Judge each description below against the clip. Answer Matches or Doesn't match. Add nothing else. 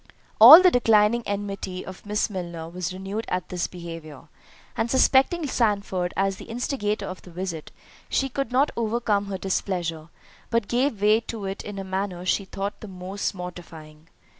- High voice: Matches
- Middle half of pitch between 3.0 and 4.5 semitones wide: Matches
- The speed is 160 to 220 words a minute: Matches